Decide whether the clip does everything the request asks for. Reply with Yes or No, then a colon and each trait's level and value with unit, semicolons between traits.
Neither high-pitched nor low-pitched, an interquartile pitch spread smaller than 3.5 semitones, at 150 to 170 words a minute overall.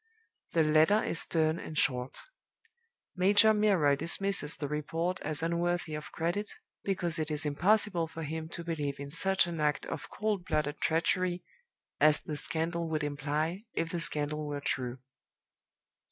Yes: medium, 160 Hz; average, 2.7 semitones; average, 155 wpm